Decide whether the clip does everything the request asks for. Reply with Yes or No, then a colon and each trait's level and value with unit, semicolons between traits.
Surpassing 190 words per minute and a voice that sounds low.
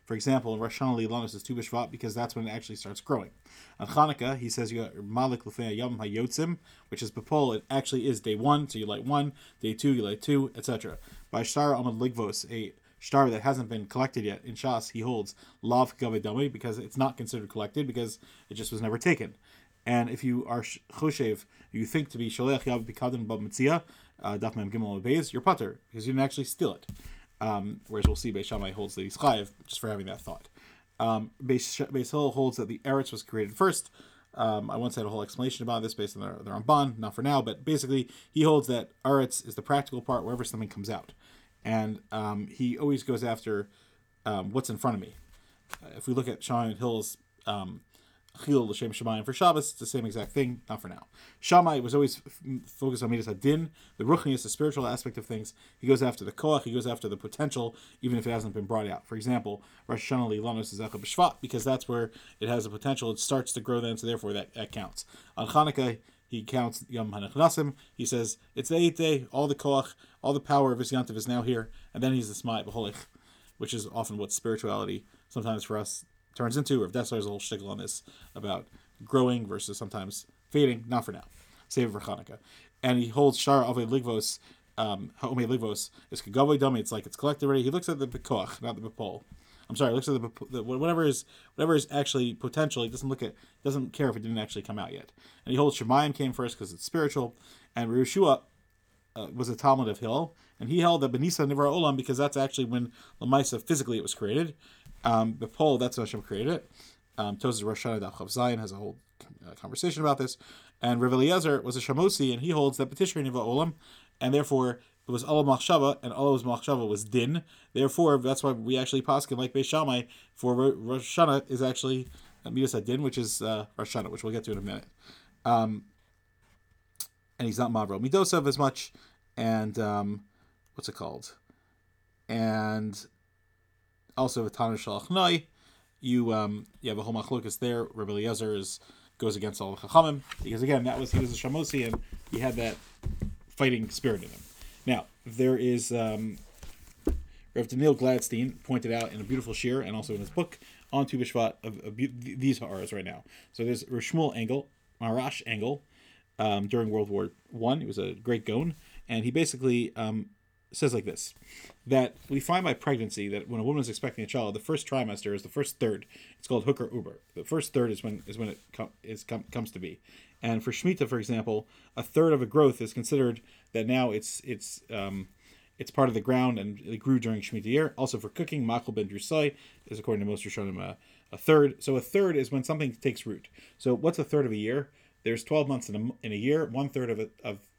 Yes: fast, 205 wpm; low, 120 Hz